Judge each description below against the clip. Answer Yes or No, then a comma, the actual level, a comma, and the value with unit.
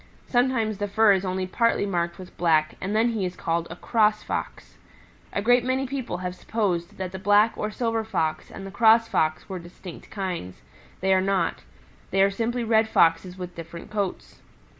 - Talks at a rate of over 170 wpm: Yes, average, 190 wpm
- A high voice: Yes, high, 195 Hz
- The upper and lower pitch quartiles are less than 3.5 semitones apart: No, average, 3.8 semitones